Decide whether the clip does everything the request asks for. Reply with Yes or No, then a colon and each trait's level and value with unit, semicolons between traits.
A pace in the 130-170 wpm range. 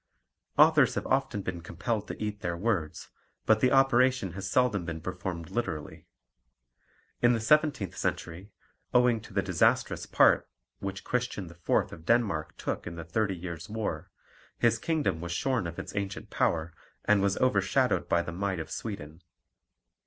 Yes: average, 160 wpm